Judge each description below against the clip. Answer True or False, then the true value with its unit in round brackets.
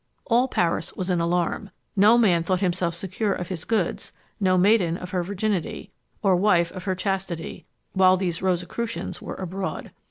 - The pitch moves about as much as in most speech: False (2.2 semitones)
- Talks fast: False (165 wpm)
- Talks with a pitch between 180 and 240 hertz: True (185 Hz)